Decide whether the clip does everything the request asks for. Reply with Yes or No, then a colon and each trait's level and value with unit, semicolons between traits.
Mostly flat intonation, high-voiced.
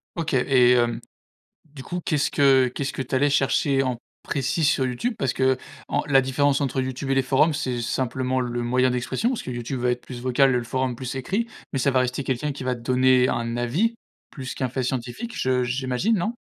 No: narrow, 2.0 semitones; low, 130 Hz